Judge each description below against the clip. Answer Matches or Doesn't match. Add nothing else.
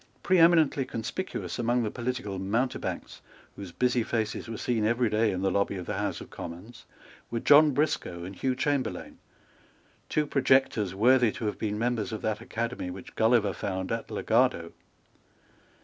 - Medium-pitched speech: Doesn't match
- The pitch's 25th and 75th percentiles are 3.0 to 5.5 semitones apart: Matches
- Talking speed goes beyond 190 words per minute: Doesn't match